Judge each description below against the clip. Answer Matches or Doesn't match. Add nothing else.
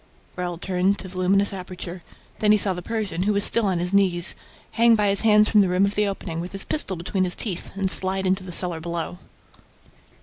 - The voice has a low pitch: Doesn't match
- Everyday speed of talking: Doesn't match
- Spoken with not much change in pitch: Matches